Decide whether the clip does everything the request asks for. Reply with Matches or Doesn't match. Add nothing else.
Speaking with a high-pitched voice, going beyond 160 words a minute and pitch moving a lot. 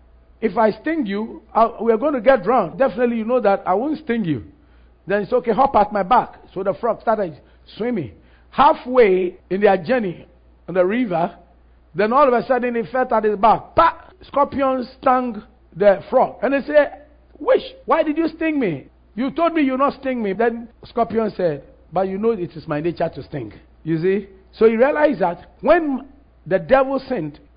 Matches